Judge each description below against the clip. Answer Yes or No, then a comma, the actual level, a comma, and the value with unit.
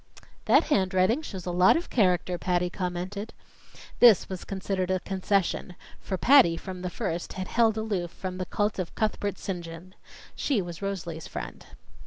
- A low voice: No, medium, 185 Hz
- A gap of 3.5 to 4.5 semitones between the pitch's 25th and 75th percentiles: No, narrow, 2.4 semitones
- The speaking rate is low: No, average, 165 wpm